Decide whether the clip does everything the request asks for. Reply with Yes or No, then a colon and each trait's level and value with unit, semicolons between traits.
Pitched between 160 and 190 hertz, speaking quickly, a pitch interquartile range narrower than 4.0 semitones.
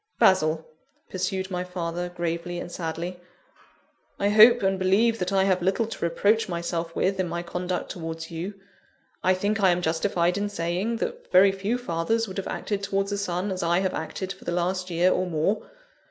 No: medium, 185 Hz; average, 190 wpm; narrow, 2.4 semitones